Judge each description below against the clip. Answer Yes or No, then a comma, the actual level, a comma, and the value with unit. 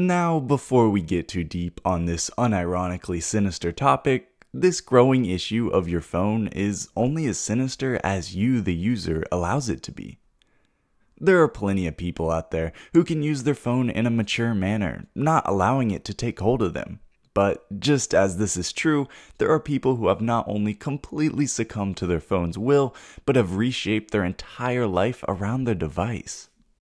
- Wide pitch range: Yes, wide, 5.9 semitones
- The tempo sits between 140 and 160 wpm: No, average, 180 wpm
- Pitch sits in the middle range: No, low, 110 Hz